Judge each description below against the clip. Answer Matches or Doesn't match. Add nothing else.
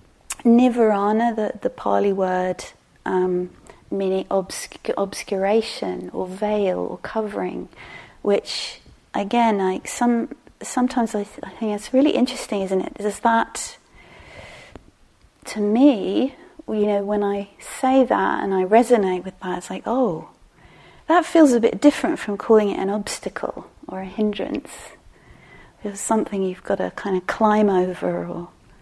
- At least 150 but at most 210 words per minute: Doesn't match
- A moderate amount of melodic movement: Matches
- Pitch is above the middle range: Matches